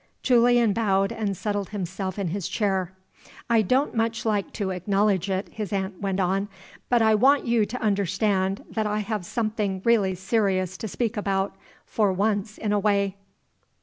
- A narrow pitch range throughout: Yes, narrow, 2.3 semitones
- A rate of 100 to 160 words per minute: No, average, 170 wpm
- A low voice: No, high, 205 Hz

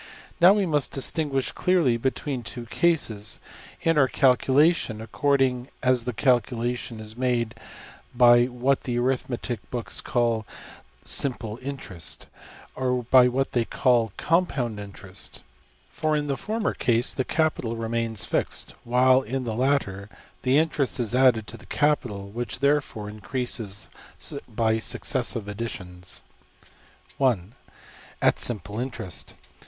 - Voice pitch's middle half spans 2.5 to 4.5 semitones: Yes, average, 3.1 semitones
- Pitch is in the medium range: No, low, 125 Hz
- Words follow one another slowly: Yes, slow, 125 wpm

